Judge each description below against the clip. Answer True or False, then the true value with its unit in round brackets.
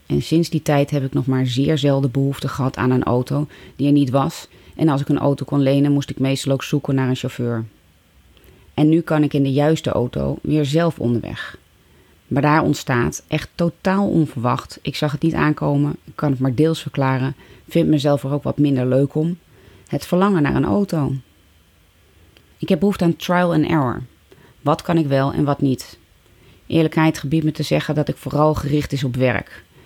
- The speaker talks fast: True (205 wpm)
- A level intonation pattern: False (3.2 semitones)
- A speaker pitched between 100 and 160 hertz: True (140 Hz)